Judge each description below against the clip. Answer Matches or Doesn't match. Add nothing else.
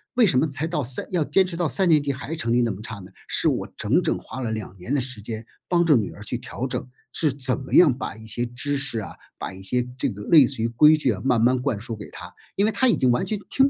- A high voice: Doesn't match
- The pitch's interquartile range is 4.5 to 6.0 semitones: Matches